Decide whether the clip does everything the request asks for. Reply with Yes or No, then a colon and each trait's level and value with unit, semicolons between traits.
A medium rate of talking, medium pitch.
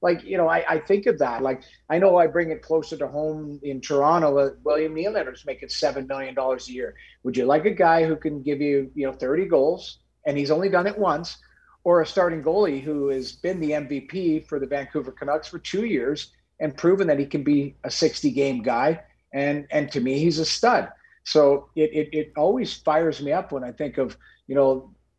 No: fast, 220 wpm; medium, 150 Hz